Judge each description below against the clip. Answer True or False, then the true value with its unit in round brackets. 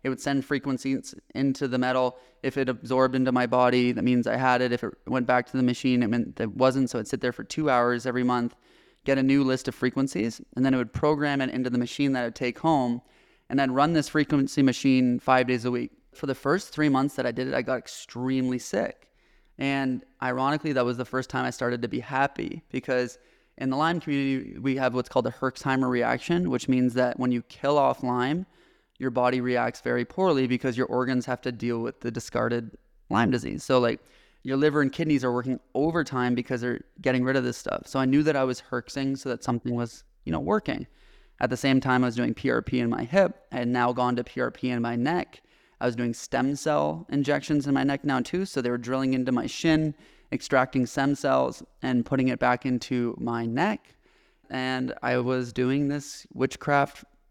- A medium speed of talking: False (225 wpm)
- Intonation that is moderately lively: False (1.7 semitones)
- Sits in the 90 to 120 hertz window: False (130 Hz)